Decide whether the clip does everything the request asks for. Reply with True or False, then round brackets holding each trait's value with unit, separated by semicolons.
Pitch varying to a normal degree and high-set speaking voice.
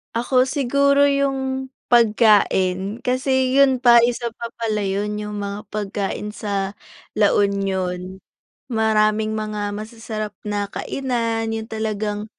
True (3.0 semitones; 215 Hz)